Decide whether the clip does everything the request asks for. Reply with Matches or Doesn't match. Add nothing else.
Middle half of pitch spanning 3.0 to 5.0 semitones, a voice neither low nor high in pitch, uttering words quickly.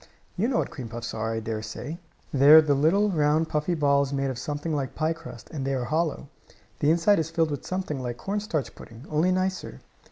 Matches